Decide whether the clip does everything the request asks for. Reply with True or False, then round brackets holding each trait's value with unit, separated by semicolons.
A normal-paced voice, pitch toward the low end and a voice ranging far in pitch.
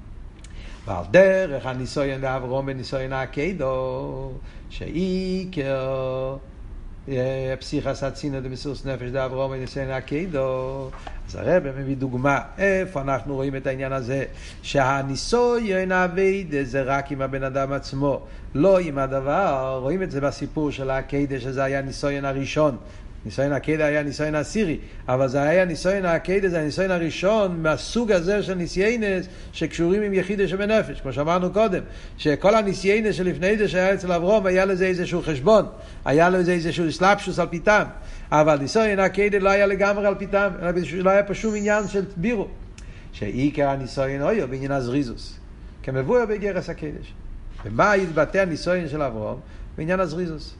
False (140 wpm; 145 Hz; 5.8 semitones)